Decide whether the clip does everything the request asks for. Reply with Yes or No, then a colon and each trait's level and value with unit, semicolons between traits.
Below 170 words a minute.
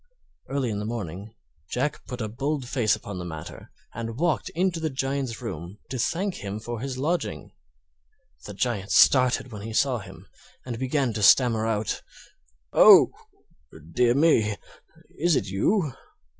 Yes: average, 155 wpm